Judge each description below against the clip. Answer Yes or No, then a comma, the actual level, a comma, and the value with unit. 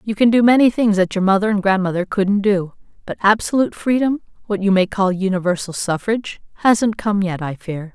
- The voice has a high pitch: Yes, high, 200 Hz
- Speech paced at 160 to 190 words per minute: Yes, average, 180 wpm